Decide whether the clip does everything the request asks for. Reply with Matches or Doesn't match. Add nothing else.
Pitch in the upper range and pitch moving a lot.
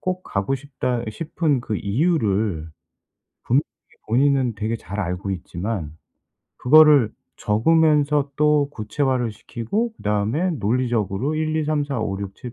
Doesn't match